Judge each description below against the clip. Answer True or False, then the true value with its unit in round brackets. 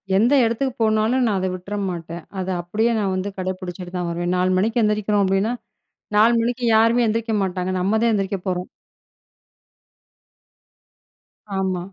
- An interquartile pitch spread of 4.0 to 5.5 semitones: False (3.3 semitones)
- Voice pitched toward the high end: True (200 Hz)